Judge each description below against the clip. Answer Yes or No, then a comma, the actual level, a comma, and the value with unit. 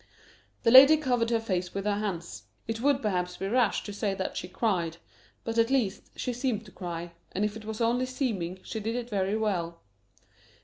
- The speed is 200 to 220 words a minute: Yes, fast, 205 wpm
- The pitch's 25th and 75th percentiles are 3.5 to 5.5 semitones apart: Yes, average, 3.9 semitones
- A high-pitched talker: Yes, high, 215 Hz